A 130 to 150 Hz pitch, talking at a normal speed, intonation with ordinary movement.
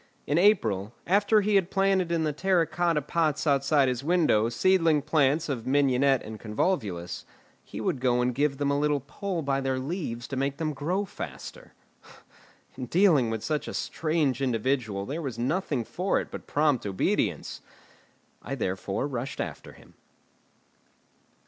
Yes: medium, 140 Hz; average, 160 wpm; average, 5.0 semitones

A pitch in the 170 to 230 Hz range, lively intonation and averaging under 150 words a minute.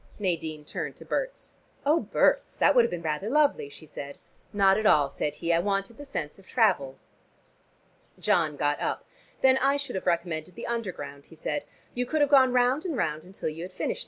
No: high, 190 Hz; wide, 8.2 semitones; fast, 205 wpm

